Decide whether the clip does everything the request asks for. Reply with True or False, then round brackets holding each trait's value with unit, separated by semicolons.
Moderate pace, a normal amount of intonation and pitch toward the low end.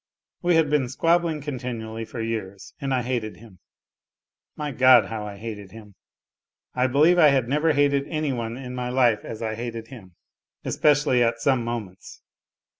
True (170 wpm; 4.0 semitones; 125 Hz)